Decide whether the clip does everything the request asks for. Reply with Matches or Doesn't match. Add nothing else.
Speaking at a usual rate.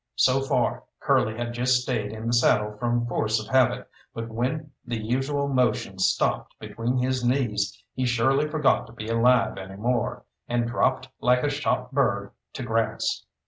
Matches